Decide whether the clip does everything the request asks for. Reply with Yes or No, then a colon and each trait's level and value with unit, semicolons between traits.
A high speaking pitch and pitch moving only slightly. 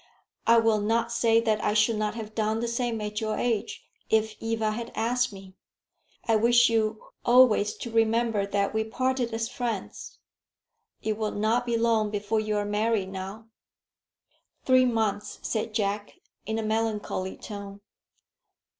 Yes: high, 220 Hz; narrow, 1.6 semitones